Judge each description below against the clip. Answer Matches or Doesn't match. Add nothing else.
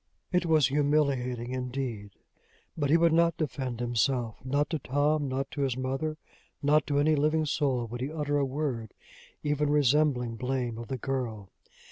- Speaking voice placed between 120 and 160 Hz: Matches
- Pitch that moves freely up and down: Doesn't match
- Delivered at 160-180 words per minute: Matches